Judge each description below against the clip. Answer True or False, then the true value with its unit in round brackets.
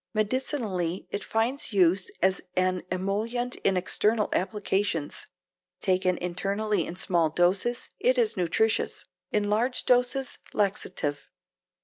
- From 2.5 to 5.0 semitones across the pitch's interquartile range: True (3.5 semitones)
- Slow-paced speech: True (110 wpm)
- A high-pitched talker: True (200 Hz)